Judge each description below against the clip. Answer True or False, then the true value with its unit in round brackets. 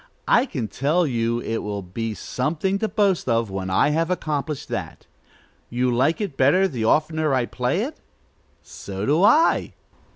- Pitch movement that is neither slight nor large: False (6.4 semitones)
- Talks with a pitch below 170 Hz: True (140 Hz)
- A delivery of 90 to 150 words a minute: False (165 wpm)